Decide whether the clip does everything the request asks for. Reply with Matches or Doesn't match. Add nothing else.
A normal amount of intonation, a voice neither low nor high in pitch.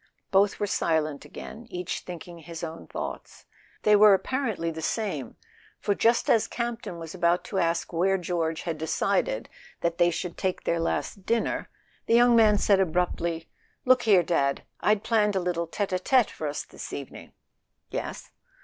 Matches